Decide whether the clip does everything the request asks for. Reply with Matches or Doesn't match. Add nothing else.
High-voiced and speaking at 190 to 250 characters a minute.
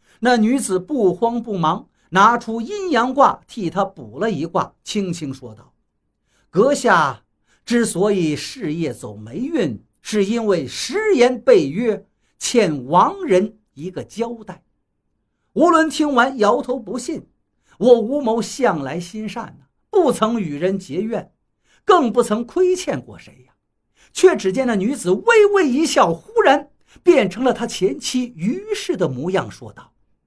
Matches